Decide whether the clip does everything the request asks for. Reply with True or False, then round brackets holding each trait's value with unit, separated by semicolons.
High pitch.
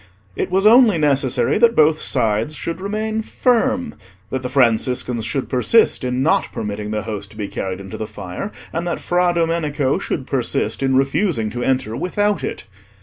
False (135 Hz)